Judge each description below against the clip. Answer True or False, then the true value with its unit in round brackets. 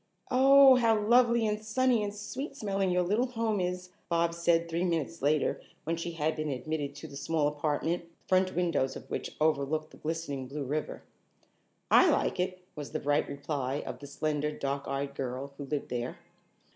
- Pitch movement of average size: True (5.0 semitones)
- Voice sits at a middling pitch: True (165 Hz)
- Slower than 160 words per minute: False (185 wpm)